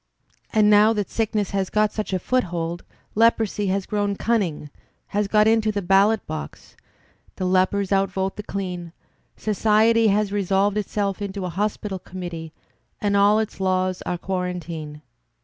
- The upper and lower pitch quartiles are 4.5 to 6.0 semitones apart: No, narrow, 2.4 semitones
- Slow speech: No, average, 150 wpm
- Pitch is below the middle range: No, high, 200 Hz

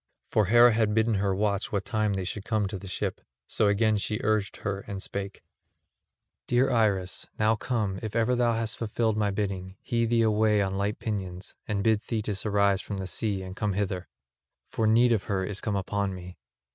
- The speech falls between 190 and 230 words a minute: Yes, average, 200 wpm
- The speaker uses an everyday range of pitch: No, narrow, 2.2 semitones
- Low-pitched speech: Yes, low, 105 Hz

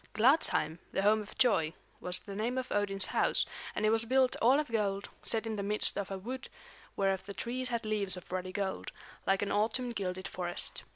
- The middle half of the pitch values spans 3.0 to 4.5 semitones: Yes, average, 3.4 semitones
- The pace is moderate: No, fast, 210 wpm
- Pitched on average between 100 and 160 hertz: No, high, 205 Hz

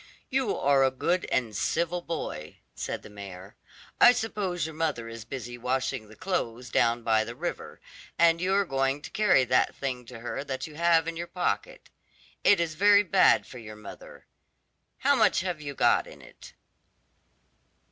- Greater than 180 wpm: No, average, 175 wpm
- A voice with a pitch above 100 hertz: Yes, medium, 140 Hz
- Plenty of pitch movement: Yes, wide, 6.7 semitones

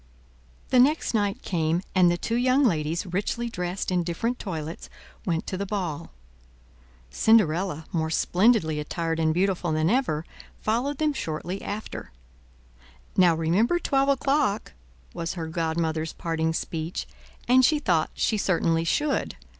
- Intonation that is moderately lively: No, wide, 6.0 semitones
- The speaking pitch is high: No, medium, 180 Hz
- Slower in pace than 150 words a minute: Yes, average, 140 wpm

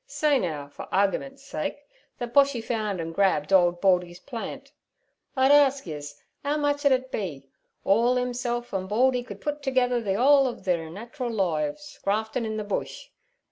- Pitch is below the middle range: No, high, 230 Hz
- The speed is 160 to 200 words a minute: Yes, average, 175 wpm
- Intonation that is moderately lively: No, wide, 6.1 semitones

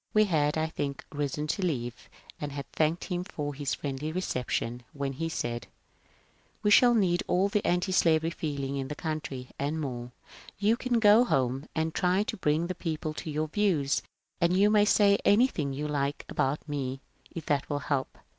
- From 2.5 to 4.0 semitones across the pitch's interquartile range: No, average, 4.6 semitones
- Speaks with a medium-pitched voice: Yes, medium, 155 Hz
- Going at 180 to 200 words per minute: Yes, average, 195 wpm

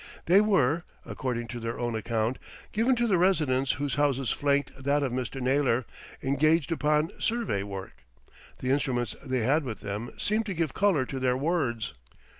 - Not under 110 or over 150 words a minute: No, average, 170 wpm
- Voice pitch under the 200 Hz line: Yes, low, 135 Hz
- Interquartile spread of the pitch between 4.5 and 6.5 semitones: Yes, average, 4.8 semitones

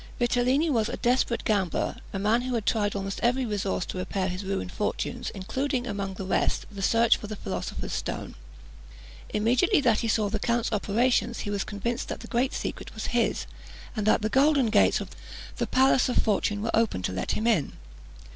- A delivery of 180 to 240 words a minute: Yes, average, 195 wpm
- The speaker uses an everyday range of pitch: Yes, average, 3.3 semitones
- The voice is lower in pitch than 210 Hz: No, high, 220 Hz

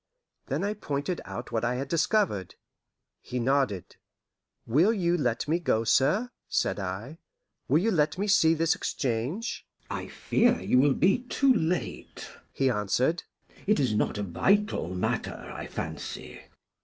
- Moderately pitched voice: Yes, medium, 150 Hz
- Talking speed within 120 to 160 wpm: Yes, average, 150 wpm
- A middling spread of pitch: No, wide, 8.1 semitones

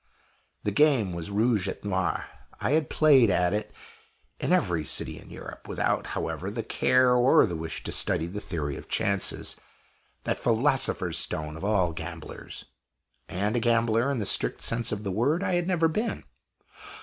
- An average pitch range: No, wide, 6.0 semitones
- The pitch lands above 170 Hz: No, low, 105 Hz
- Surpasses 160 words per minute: Yes, average, 175 wpm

